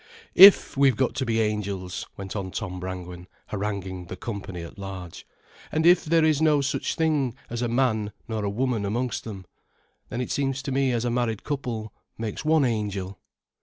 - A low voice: Yes, low, 110 Hz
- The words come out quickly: No, average, 185 wpm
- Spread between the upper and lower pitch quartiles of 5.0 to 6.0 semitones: Yes, average, 5.3 semitones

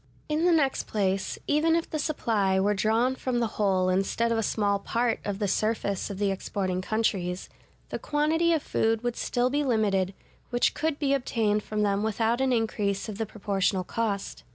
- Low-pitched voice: No, high, 220 Hz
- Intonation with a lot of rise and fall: No, average, 4.2 semitones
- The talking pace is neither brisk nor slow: Yes, average, 190 wpm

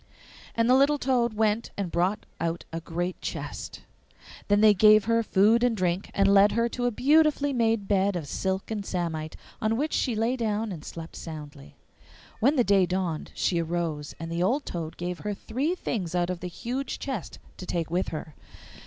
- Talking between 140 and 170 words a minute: No, average, 195 wpm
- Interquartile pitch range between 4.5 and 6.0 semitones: Yes, average, 5.1 semitones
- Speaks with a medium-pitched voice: No, high, 200 Hz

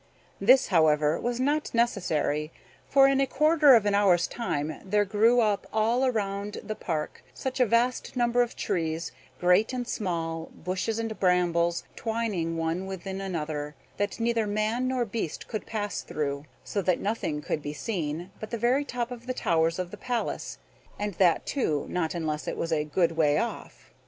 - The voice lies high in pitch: Yes, high, 200 Hz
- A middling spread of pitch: No, wide, 6.1 semitones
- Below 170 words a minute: No, average, 180 wpm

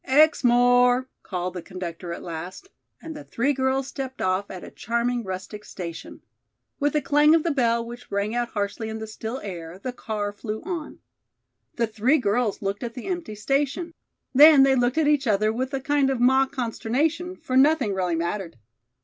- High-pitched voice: Yes, high, 240 Hz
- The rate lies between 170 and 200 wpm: Yes, average, 185 wpm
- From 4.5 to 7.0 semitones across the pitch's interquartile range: Yes, average, 5.0 semitones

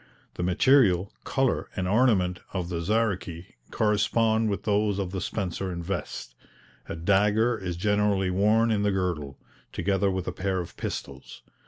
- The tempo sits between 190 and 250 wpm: No, average, 155 wpm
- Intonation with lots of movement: No, average, 2.8 semitones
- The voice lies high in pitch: No, low, 100 Hz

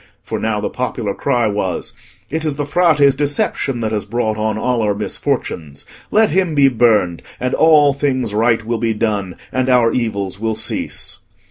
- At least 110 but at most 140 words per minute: No, average, 175 wpm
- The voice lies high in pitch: No, low, 115 Hz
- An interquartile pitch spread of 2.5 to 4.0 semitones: No, average, 4.7 semitones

